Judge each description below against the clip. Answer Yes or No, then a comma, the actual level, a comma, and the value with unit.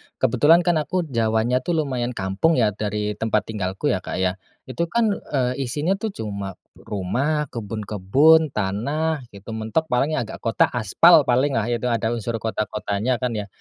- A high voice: No, low, 120 Hz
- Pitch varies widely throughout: Yes, wide, 6.0 semitones